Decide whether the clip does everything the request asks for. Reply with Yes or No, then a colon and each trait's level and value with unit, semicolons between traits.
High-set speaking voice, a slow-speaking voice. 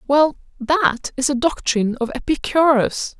Yes: very high, 270 Hz; slow, 130 wpm